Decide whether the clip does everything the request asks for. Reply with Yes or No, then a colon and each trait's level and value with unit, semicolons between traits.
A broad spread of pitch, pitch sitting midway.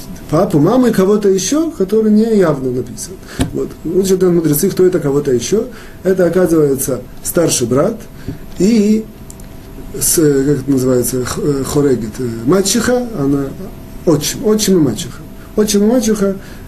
Yes: wide, 7.5 semitones; medium, 175 Hz